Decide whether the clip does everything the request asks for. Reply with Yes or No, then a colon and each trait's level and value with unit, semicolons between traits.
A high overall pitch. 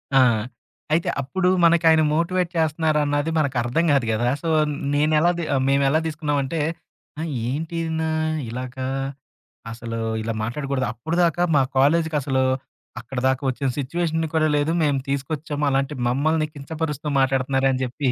No: medium, 145 Hz